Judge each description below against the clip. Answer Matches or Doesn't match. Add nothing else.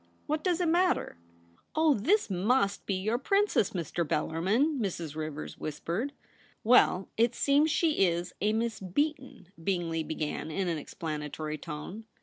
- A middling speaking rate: Matches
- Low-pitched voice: Doesn't match